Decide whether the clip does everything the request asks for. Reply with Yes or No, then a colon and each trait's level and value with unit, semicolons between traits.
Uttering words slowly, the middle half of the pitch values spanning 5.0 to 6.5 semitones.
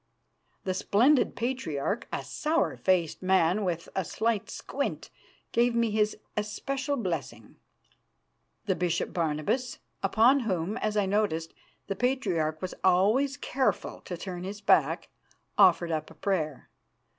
Yes: slow, 130 wpm; wide, 5.5 semitones